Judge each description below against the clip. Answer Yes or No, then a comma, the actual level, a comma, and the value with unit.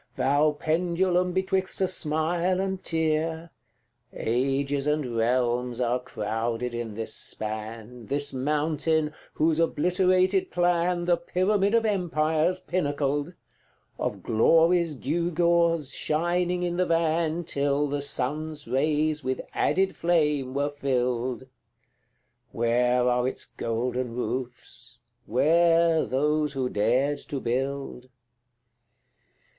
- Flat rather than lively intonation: No, average, 5.1 semitones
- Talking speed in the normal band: No, slow, 105 wpm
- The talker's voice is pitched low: No, medium, 150 Hz